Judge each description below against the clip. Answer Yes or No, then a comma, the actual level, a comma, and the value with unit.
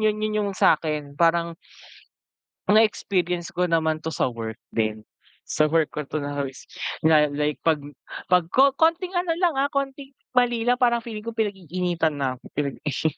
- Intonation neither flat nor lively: No, wide, 7.5 semitones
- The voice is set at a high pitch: No, medium, 170 Hz